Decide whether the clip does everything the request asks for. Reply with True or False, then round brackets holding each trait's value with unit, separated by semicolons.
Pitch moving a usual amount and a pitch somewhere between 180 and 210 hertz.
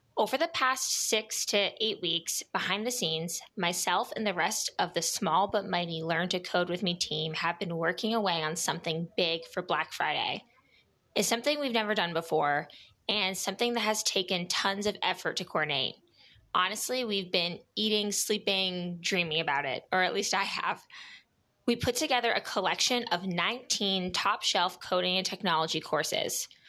True (4.1 semitones; 190 Hz)